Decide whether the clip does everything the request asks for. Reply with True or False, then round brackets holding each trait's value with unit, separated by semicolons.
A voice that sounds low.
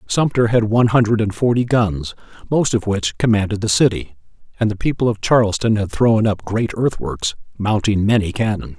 True (105 Hz)